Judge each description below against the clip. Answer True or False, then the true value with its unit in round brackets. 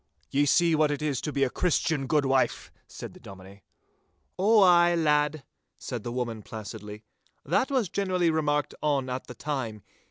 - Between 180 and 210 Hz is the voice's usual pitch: False (145 Hz)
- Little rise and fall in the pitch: False (4.9 semitones)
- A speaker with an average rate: True (170 wpm)